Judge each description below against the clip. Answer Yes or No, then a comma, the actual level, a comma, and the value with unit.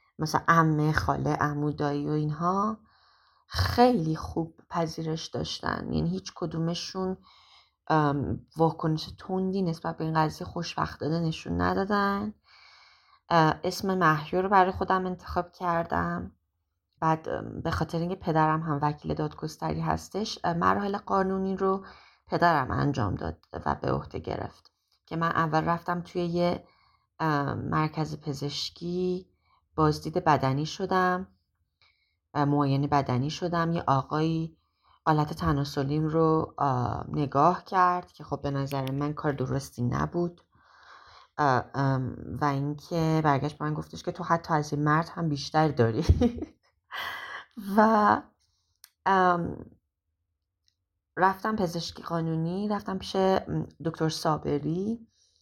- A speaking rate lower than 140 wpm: Yes, slow, 105 wpm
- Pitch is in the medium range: Yes, medium, 160 Hz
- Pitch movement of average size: Yes, average, 3.9 semitones